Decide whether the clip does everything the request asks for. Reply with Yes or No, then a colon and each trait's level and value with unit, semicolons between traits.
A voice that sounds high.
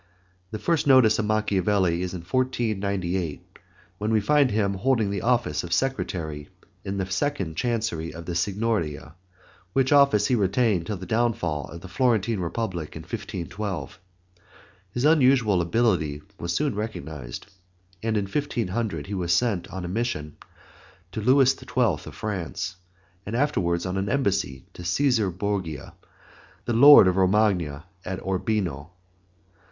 No: low, 100 Hz